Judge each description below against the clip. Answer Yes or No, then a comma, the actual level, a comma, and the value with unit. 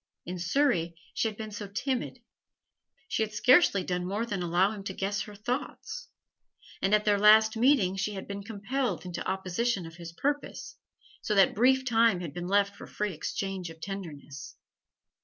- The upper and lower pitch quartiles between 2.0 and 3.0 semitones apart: No, average, 3.7 semitones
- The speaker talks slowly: No, average, 175 wpm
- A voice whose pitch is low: No, high, 200 Hz